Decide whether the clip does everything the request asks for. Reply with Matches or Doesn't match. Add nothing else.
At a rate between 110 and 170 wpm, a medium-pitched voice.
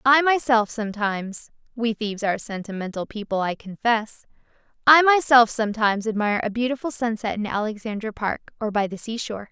Doesn't match